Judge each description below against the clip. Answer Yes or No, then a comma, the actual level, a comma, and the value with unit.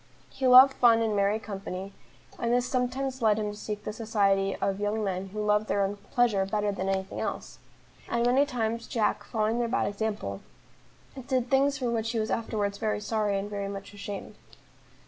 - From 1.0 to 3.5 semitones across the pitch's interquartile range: Yes, average, 2.8 semitones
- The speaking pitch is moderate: No, high, 215 Hz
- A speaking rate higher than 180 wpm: Yes, average, 195 wpm